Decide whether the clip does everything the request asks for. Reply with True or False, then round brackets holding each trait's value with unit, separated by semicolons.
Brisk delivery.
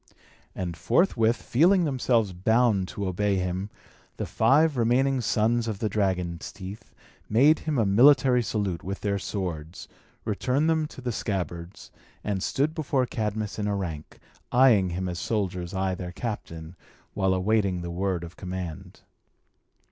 False (150 wpm)